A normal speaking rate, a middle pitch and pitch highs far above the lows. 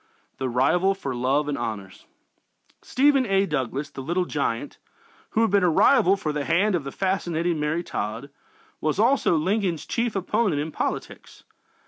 Yes: average, 160 wpm; medium, 165 Hz; wide, 5.7 semitones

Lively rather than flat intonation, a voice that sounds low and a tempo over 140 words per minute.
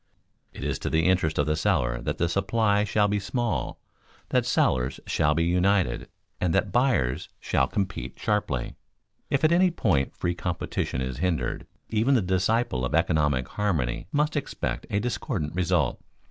Yes: wide, 6.0 semitones; very low, 90 Hz; average, 160 wpm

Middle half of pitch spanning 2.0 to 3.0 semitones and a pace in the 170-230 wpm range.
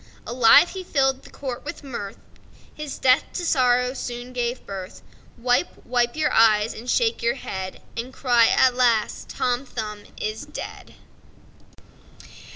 No: narrow, 2.5 semitones; slow, 135 wpm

